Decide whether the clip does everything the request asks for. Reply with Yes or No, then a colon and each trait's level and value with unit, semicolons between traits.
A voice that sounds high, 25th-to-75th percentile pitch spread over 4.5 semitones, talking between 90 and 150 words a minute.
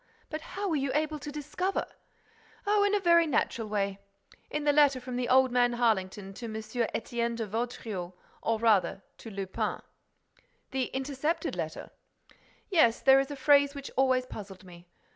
No: very high, 255 Hz; average, 5.1 semitones; average, 160 wpm